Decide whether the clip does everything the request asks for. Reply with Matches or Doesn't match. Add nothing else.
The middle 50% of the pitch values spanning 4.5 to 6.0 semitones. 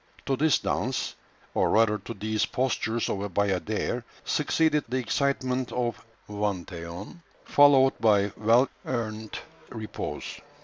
Doesn't match